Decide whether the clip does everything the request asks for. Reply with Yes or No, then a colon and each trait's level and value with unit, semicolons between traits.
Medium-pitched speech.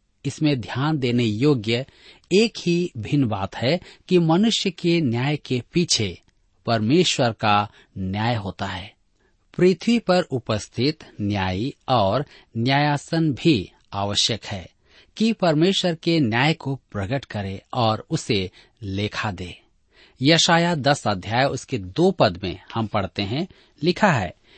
No: low, 130 Hz